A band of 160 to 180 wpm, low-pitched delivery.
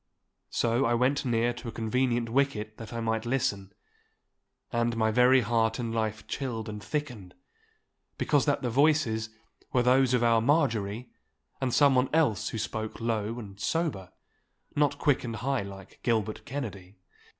No: average, 150 wpm; low, 115 Hz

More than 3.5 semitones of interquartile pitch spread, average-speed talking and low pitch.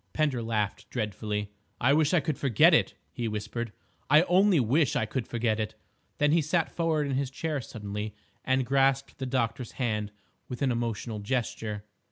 Yes: average, 4.6 semitones; average, 175 wpm; low, 125 Hz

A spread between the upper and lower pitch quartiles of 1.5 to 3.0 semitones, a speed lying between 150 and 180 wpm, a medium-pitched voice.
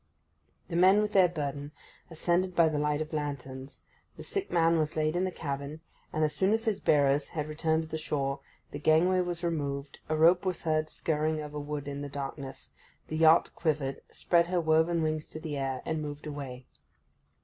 No: average, 2.7 semitones; average, 195 wpm; medium, 155 Hz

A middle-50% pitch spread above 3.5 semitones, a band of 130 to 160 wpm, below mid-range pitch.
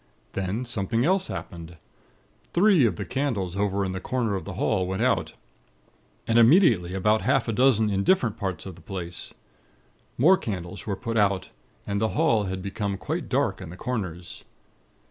No: average, 4.4 semitones; average, 175 wpm; low, 105 Hz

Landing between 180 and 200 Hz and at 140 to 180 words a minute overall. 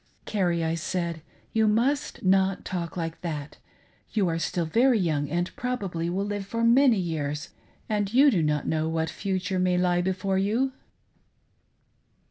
Yes: medium, 185 Hz; average, 155 wpm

